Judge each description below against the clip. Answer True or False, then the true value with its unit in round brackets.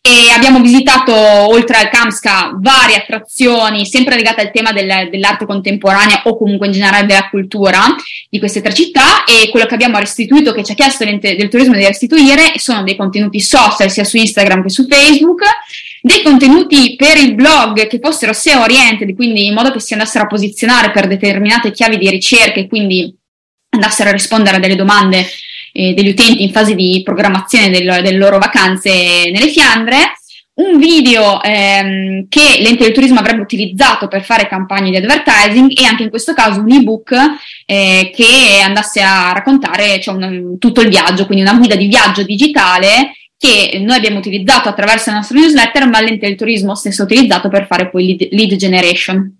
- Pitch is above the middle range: True (215 Hz)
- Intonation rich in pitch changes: False (4.0 semitones)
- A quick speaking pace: True (180 wpm)